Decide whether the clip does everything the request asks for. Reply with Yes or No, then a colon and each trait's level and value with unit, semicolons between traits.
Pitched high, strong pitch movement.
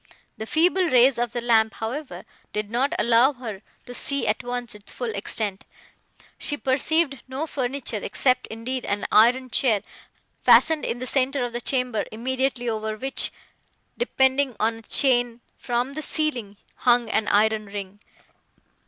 No: high, 245 Hz; average, 3.3 semitones